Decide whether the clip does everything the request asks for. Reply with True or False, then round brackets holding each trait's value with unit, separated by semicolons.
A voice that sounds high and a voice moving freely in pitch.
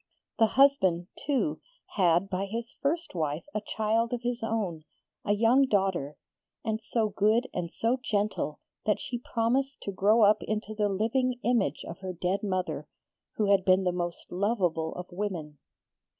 False (210 Hz; 4.1 semitones)